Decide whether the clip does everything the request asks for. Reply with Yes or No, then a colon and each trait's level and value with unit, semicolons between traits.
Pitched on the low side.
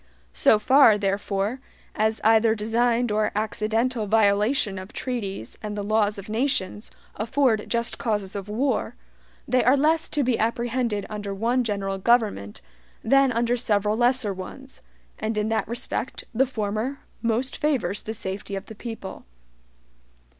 No: high, 220 Hz